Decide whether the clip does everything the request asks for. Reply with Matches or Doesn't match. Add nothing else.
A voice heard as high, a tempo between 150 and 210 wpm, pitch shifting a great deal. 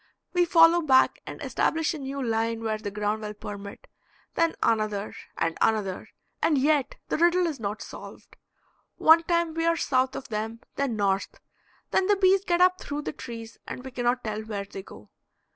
Matches